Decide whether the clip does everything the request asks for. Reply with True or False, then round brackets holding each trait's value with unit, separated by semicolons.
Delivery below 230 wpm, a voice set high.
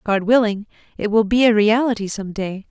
True (200 wpm; 215 Hz)